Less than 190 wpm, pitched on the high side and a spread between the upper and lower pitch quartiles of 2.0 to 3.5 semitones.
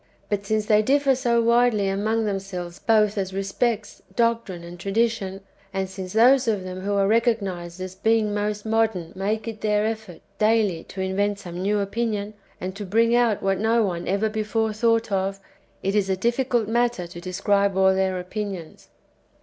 Yes: average, 180 wpm; high, 205 Hz; average, 2.8 semitones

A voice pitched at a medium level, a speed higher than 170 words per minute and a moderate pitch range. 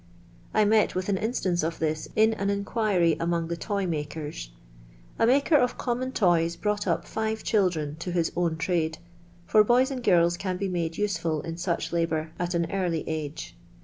Yes: medium, 175 Hz; average, 180 wpm; average, 4.2 semitones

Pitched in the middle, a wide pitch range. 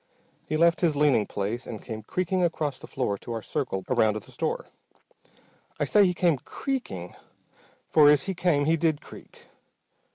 Yes: medium, 145 Hz; wide, 7.5 semitones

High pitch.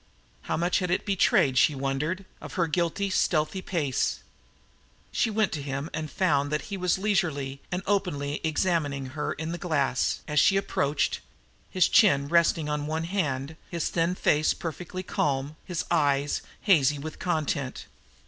No: medium, 155 Hz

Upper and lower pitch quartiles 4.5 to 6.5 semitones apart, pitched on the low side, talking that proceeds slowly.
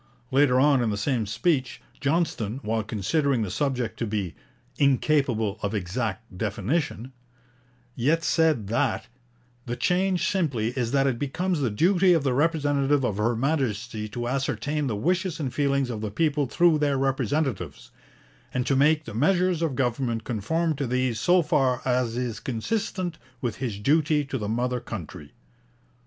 No: average, 4.9 semitones; low, 130 Hz; average, 160 wpm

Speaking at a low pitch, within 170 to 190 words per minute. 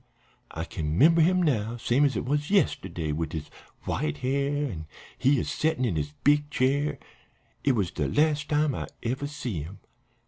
Yes: low, 130 Hz; average, 180 wpm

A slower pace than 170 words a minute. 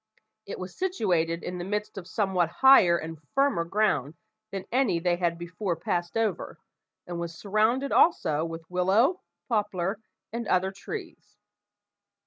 Yes: average, 140 wpm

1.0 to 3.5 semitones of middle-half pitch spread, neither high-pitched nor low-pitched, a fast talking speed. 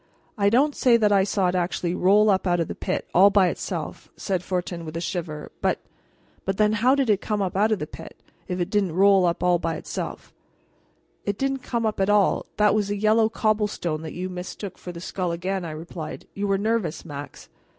No: average, 3.1 semitones; high, 195 Hz; fast, 225 wpm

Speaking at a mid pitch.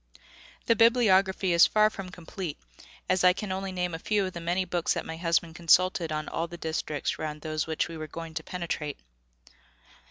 Yes: medium, 175 Hz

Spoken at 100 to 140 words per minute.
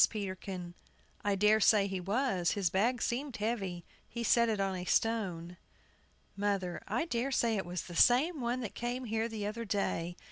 No: average, 180 wpm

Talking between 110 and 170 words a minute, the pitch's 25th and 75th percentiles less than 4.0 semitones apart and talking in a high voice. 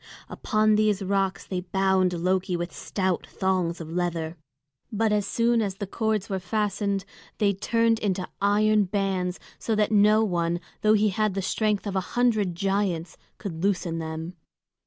Yes: average, 160 wpm; average, 2.9 semitones; high, 195 Hz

